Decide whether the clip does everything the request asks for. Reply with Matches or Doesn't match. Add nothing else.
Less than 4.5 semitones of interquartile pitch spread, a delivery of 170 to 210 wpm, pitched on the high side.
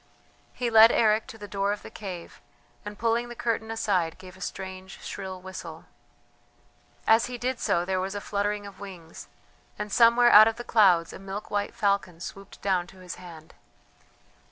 Matches